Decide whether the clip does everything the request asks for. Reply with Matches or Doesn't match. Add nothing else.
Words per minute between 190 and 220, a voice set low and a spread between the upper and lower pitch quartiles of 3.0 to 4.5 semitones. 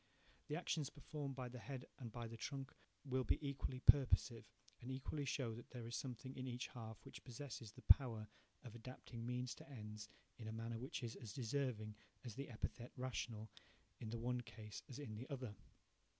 Doesn't match